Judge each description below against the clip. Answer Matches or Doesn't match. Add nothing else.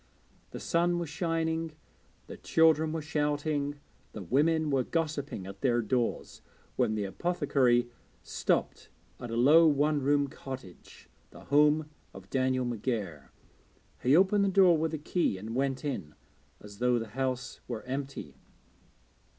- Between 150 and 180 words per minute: Doesn't match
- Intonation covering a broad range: Doesn't match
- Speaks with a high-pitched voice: Doesn't match